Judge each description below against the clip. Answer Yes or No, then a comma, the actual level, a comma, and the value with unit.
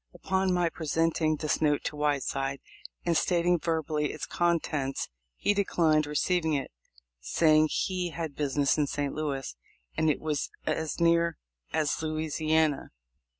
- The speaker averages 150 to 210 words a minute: No, slow, 135 wpm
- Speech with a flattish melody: Yes, narrow, 2.3 semitones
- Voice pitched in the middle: Yes, medium, 155 Hz